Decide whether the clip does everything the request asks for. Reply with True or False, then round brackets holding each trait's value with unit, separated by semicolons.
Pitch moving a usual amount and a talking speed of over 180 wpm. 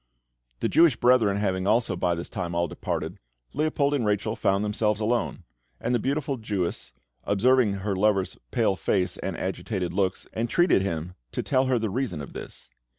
False (4.6 semitones; 170 wpm)